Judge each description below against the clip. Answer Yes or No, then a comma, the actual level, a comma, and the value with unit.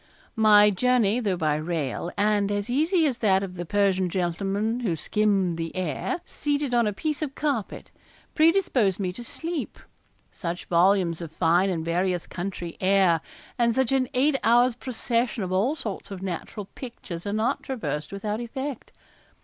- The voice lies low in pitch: No, high, 205 Hz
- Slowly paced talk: No, average, 165 wpm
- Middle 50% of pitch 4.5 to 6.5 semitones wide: Yes, wide, 5.5 semitones